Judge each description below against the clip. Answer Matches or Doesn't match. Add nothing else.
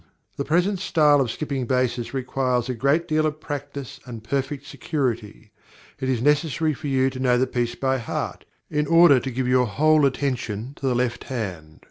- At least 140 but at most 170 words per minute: Doesn't match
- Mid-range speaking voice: Doesn't match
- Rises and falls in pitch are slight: Doesn't match